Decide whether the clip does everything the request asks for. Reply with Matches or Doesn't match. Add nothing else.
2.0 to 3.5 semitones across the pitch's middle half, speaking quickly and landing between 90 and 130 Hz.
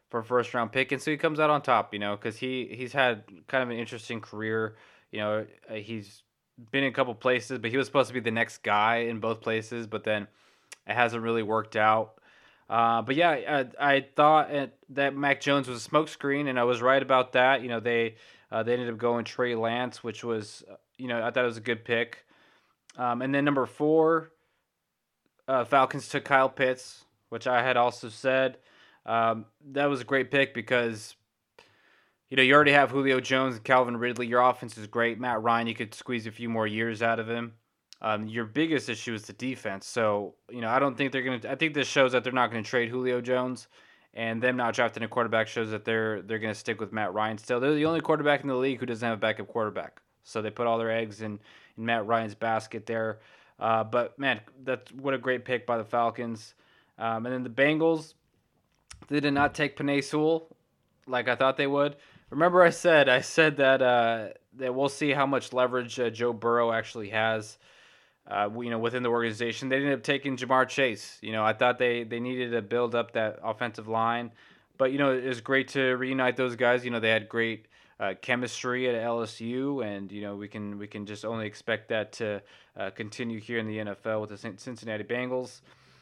Matches